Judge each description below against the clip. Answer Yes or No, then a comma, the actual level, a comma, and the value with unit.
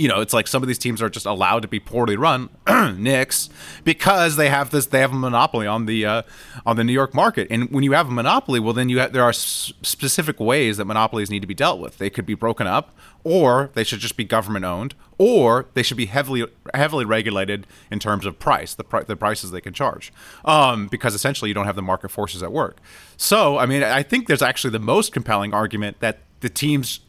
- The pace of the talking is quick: Yes, fast, 240 wpm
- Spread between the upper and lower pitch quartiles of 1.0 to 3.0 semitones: No, average, 3.6 semitones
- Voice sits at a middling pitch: No, low, 115 Hz